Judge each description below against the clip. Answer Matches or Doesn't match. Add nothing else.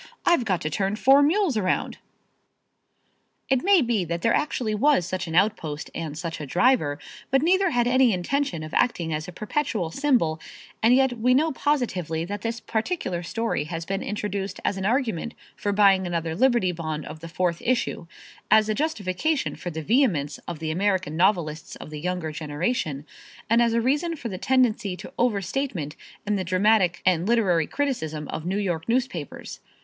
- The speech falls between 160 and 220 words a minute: Matches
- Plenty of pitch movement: Matches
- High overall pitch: Matches